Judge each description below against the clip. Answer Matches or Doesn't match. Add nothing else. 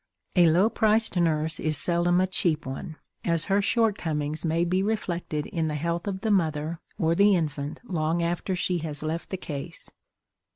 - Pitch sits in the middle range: Matches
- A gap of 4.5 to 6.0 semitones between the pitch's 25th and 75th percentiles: Doesn't match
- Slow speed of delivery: Doesn't match